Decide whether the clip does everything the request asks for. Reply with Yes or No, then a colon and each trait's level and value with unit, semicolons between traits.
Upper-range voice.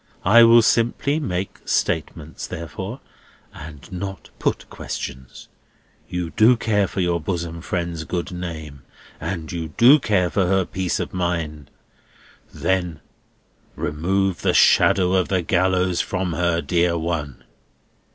No: very low, 90 Hz